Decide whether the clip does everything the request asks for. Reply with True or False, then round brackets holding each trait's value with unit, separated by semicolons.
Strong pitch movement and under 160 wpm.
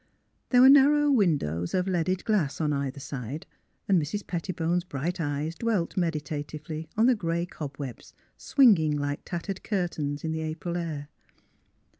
False (4.2 semitones; 150 wpm)